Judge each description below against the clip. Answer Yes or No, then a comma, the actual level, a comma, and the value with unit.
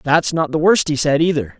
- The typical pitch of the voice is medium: Yes, medium, 155 Hz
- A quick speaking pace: Yes, fast, 265 wpm